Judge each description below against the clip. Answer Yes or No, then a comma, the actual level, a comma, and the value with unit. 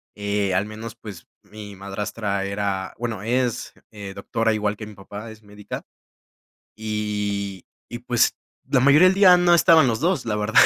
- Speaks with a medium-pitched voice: No, low, 105 Hz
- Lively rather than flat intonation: No, narrow, 2.6 semitones